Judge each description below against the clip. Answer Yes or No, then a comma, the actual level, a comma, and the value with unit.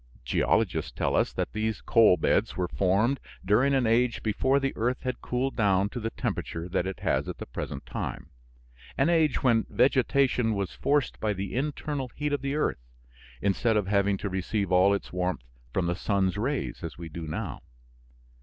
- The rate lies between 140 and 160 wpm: No, average, 185 wpm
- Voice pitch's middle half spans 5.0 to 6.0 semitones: Yes, wide, 5.5 semitones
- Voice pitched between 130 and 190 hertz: No, low, 110 Hz